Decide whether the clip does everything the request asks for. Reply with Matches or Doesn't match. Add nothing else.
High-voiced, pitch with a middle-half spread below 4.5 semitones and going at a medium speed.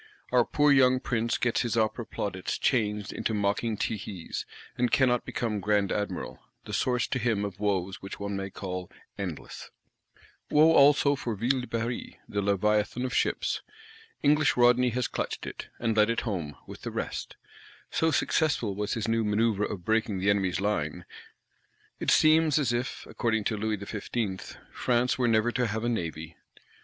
Doesn't match